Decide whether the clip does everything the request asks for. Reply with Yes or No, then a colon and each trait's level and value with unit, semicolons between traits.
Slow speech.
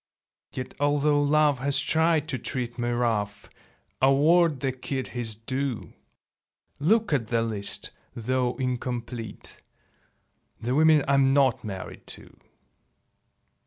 Yes: slow, 115 wpm